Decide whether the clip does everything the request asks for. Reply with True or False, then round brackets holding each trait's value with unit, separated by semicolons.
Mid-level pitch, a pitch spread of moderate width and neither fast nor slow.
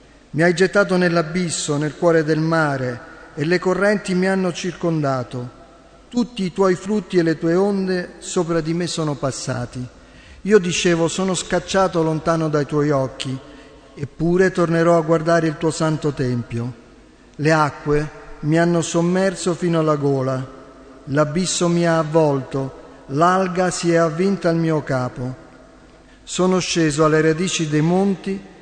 True (165 Hz; 3.5 semitones; 145 wpm)